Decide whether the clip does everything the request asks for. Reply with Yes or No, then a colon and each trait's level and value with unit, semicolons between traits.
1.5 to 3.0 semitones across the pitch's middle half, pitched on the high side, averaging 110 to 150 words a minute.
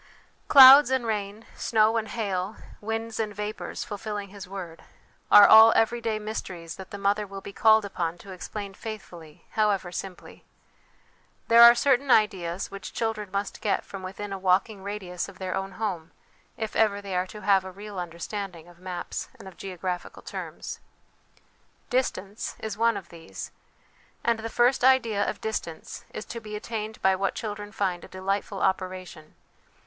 No: average, 2.7 semitones; high, 200 Hz; average, 165 wpm